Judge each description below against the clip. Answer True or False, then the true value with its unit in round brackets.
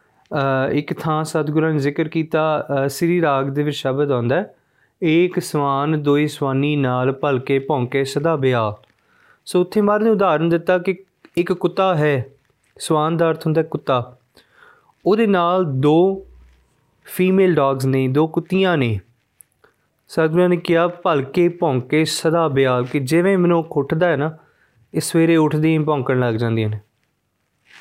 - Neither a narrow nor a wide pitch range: True (4.2 semitones)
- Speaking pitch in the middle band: True (155 Hz)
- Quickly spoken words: False (140 wpm)